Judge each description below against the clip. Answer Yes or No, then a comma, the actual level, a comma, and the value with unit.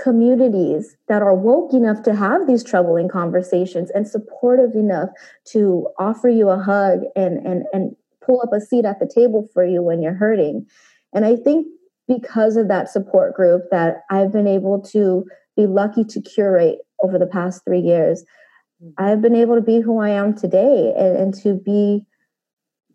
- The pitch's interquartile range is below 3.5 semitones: No, average, 4.0 semitones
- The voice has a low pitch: No, high, 205 Hz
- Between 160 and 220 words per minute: Yes, average, 180 wpm